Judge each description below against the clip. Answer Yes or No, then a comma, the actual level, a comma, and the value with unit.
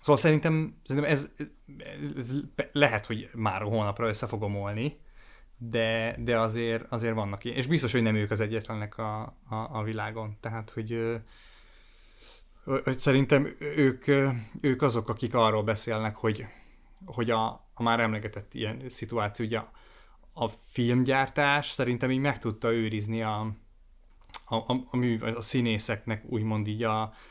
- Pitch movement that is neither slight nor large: Yes, average, 3.0 semitones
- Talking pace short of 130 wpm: No, average, 145 wpm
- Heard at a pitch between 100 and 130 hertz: Yes, low, 115 Hz